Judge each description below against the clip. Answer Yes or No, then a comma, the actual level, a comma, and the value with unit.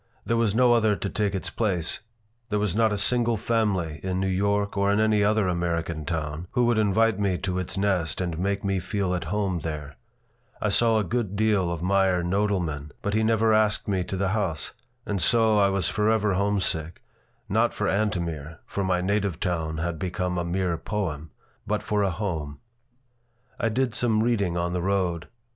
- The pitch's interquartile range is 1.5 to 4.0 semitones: Yes, average, 3.4 semitones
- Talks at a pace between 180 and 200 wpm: Yes, average, 195 wpm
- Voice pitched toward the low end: Yes, very low, 95 Hz